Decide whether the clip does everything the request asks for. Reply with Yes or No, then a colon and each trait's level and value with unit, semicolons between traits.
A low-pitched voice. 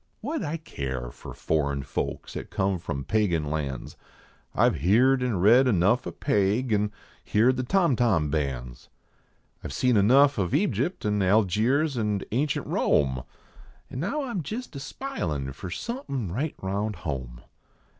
Yes: low, 105 Hz